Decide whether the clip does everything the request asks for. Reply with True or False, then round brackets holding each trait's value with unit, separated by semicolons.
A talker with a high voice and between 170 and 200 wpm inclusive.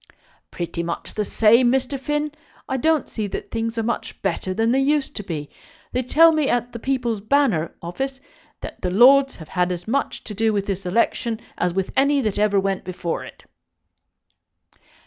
True (225 Hz; 185 wpm)